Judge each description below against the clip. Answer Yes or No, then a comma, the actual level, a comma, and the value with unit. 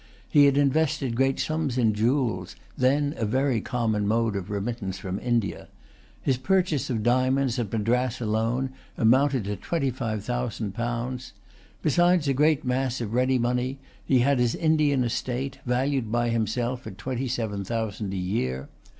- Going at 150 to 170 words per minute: Yes, average, 160 wpm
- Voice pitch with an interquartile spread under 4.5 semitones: Yes, average, 3.3 semitones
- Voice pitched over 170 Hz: No, low, 125 Hz